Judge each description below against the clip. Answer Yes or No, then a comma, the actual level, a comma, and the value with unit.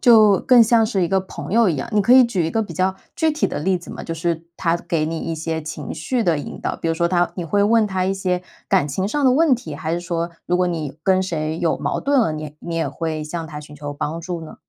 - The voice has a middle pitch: Yes, medium, 175 Hz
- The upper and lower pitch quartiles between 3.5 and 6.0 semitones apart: Yes, average, 4.1 semitones